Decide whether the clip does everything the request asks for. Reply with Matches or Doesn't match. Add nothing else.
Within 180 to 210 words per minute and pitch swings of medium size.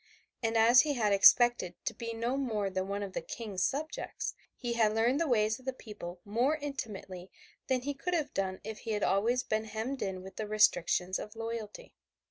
Matches